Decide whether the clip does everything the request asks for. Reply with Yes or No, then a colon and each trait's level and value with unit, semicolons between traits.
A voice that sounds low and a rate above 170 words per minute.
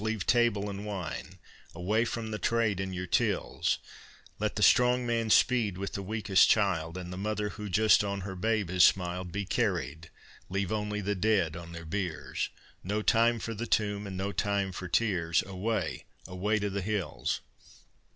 Yes: low, 100 Hz; average, 180 wpm